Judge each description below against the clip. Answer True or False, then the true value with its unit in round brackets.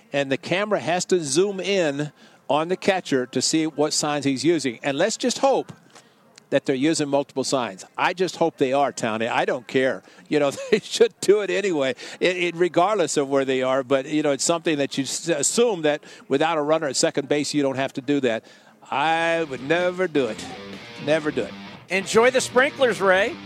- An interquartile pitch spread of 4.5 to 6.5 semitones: True (5.1 semitones)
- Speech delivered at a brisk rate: True (210 wpm)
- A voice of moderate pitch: True (150 Hz)